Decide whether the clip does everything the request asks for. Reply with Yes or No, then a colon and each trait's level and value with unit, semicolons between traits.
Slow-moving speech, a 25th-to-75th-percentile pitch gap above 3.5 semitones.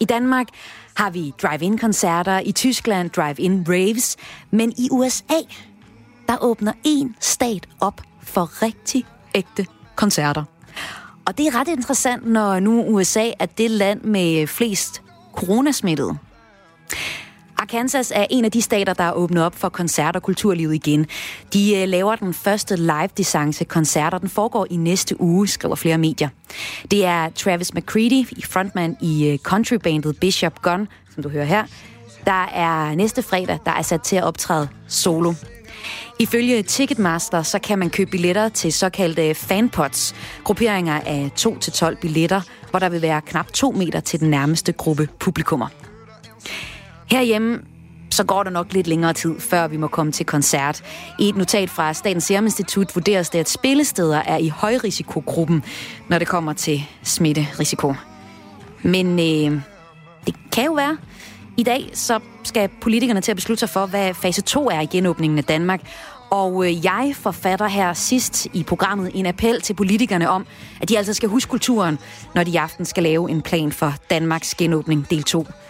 No: average, 160 wpm; average, 4.7 semitones